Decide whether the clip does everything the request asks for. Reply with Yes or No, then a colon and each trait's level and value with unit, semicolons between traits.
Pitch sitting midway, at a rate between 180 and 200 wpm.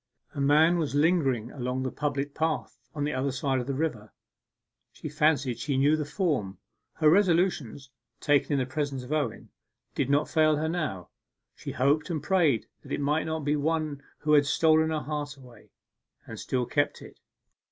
Yes: medium, 145 Hz; average, 185 wpm